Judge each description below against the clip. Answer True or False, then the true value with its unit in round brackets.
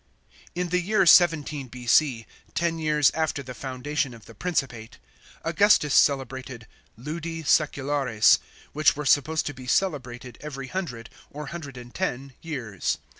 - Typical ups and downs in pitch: True (4.1 semitones)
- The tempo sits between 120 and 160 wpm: True (145 wpm)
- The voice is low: False (145 Hz)